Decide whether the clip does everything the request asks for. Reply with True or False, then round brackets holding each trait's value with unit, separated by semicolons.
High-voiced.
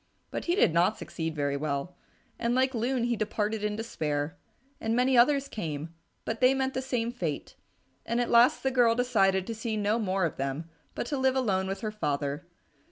True (220 Hz)